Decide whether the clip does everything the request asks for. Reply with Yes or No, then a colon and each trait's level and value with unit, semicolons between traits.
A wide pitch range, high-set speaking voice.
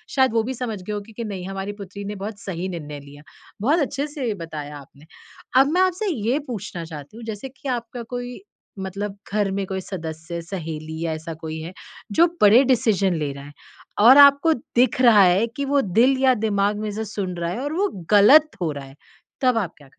Yes: wide, 6.5 semitones; high, 205 Hz